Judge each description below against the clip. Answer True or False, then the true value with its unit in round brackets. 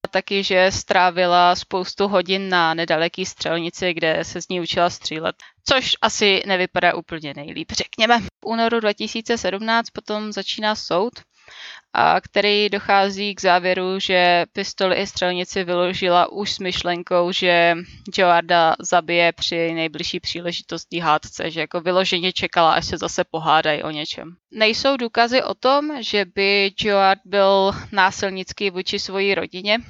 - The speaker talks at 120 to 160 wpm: True (135 wpm)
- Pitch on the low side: False (185 Hz)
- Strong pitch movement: False (2.5 semitones)